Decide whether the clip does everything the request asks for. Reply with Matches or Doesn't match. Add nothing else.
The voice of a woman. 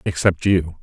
Doesn't match